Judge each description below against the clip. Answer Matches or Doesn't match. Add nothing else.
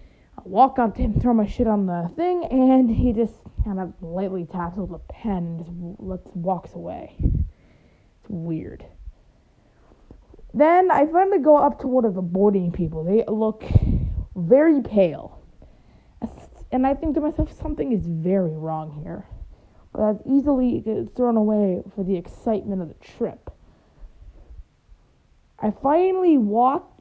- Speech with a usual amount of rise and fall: Doesn't match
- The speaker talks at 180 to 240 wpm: Doesn't match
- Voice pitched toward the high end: Matches